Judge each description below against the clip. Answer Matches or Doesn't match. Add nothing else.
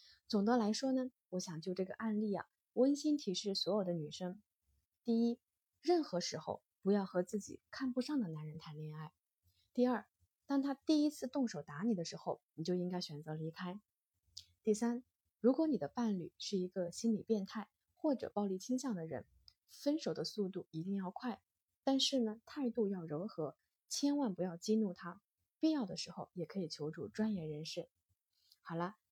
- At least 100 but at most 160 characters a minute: Doesn't match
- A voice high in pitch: Matches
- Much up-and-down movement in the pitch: Matches